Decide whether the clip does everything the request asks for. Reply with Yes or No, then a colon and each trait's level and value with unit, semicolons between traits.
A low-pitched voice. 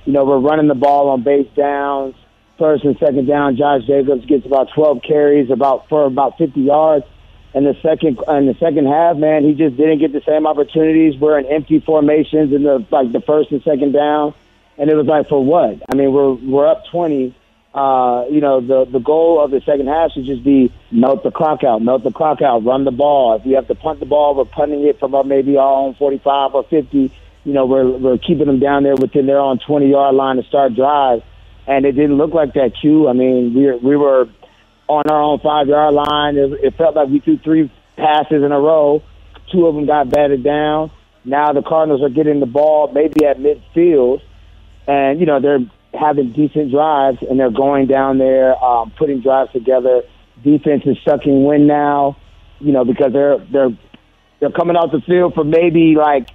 No: medium, 145 Hz